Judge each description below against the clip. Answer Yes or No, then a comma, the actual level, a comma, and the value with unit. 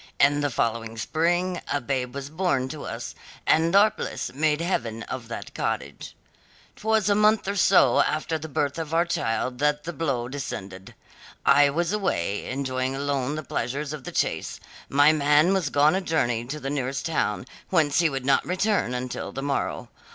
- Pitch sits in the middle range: Yes, medium, 145 Hz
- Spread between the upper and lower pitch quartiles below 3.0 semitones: No, average, 4.3 semitones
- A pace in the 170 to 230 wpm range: Yes, average, 180 wpm